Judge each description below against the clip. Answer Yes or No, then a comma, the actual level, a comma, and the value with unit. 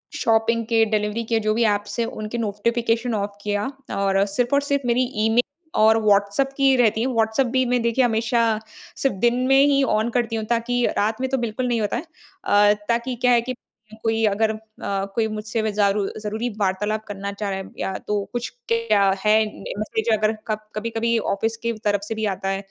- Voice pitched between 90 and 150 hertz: No, high, 220 Hz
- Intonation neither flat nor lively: No, narrow, 2.3 semitones